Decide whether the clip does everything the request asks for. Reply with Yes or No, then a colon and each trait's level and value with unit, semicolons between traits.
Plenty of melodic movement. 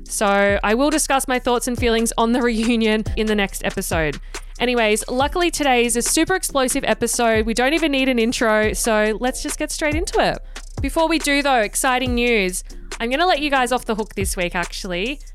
No: average, 4.3 semitones